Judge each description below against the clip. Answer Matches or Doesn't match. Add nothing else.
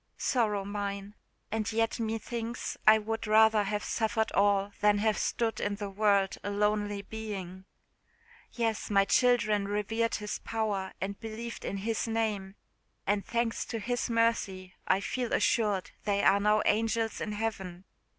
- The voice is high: Matches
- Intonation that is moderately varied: Doesn't match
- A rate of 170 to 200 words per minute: Doesn't match